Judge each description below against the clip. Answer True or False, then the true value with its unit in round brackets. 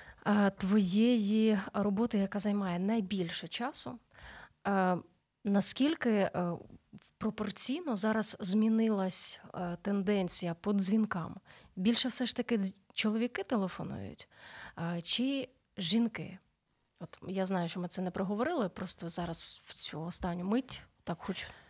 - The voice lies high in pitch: True (200 Hz)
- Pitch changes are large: False (3.4 semitones)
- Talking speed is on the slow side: True (100 wpm)